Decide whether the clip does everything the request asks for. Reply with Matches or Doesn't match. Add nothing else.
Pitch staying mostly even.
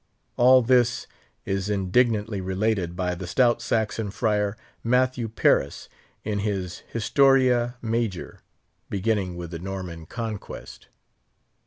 Doesn't match